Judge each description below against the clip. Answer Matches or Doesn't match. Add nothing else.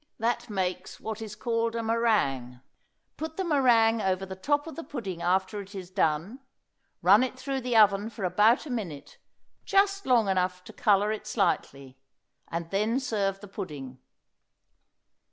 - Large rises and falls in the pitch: Doesn't match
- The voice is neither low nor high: Doesn't match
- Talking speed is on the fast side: Doesn't match